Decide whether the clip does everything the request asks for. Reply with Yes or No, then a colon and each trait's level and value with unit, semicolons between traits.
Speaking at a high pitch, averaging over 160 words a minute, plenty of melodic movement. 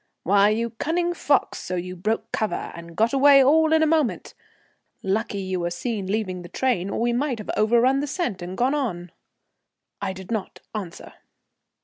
Yes: high, 220 Hz; average, 180 wpm; wide, 6.4 semitones